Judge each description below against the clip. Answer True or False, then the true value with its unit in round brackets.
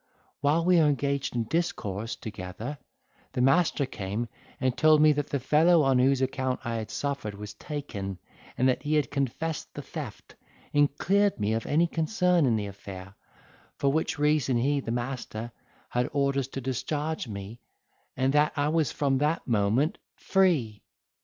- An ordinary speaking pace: True (165 wpm)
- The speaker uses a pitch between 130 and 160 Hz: True (135 Hz)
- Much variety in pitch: False (4.5 semitones)